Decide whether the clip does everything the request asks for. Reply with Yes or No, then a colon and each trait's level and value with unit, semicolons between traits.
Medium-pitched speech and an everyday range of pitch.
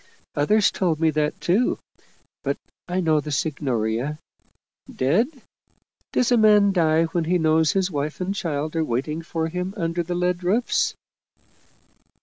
Yes: medium, 165 Hz; average, 3.2 semitones